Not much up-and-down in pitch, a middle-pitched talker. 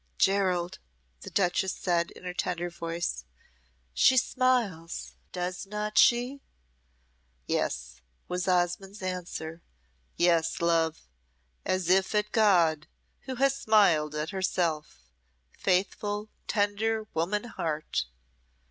No: average, 3.8 semitones; medium, 180 Hz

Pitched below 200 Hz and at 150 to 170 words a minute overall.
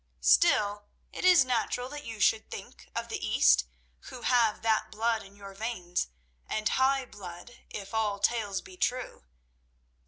No: high, 220 Hz; average, 155 wpm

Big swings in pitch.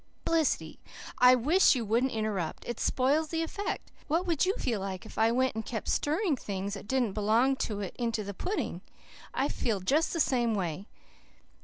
Yes: wide, 5.9 semitones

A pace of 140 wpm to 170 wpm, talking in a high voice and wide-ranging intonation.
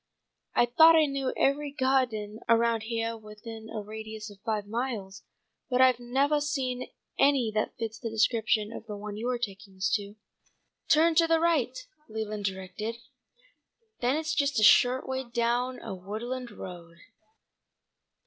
No: average, 150 wpm; high, 230 Hz; average, 3.5 semitones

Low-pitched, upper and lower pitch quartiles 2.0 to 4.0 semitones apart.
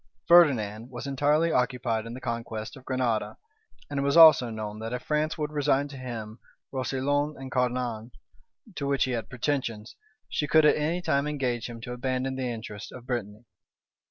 Yes: low, 130 Hz; average, 3.5 semitones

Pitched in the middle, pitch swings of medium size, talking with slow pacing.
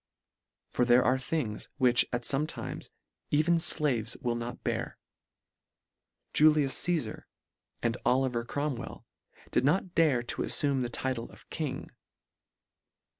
No: low, 130 Hz; average, 3.9 semitones; slow, 125 wpm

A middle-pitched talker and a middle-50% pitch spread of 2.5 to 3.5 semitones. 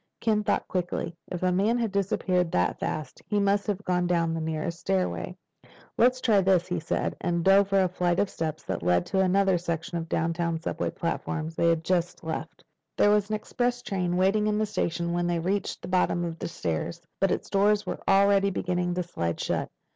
Yes: medium, 180 Hz; average, 3.0 semitones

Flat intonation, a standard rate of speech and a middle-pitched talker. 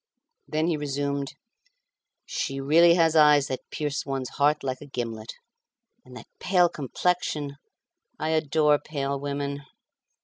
No: narrow, 2.3 semitones; slow, 130 wpm; medium, 145 Hz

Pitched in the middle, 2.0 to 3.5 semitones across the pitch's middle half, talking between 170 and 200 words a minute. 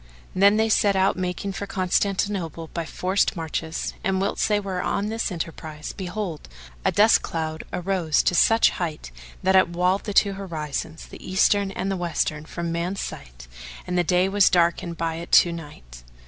Yes: medium, 180 Hz; average, 3.1 semitones; average, 175 wpm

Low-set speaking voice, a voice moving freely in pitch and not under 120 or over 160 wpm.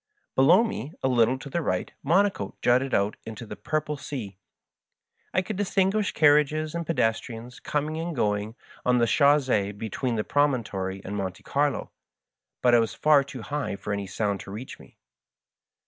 No: low, 130 Hz; wide, 6.0 semitones; average, 170 wpm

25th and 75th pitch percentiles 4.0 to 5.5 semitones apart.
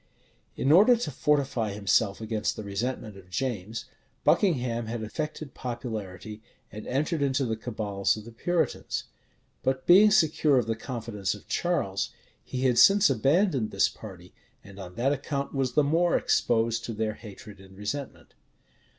Yes: average, 4.9 semitones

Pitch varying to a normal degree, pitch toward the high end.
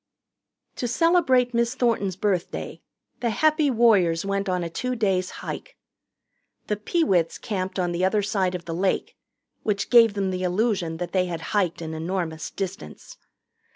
Yes: average, 4.5 semitones; high, 195 Hz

